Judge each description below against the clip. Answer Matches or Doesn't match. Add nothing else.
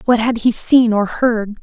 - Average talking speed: Doesn't match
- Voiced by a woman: Matches